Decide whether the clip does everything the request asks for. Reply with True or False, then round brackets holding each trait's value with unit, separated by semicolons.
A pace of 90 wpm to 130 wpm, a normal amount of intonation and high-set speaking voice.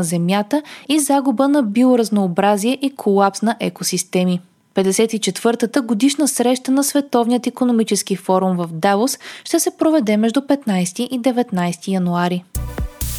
False (120 wpm; 5.9 semitones; 225 Hz)